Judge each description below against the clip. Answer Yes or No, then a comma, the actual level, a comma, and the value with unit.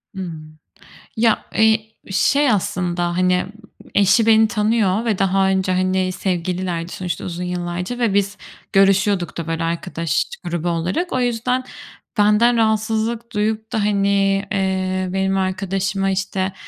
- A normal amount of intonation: Yes, average, 3.0 semitones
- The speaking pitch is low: No, high, 195 Hz